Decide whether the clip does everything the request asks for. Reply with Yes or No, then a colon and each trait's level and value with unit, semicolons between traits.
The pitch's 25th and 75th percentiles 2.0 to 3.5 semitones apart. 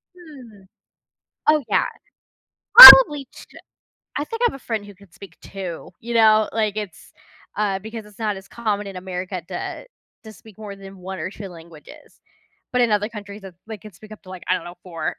Yes: average, 2.7 semitones